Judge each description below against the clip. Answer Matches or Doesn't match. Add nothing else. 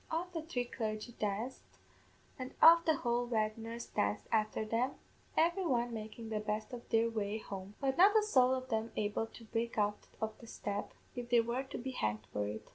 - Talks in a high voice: Matches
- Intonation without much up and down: Doesn't match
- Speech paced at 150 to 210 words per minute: Matches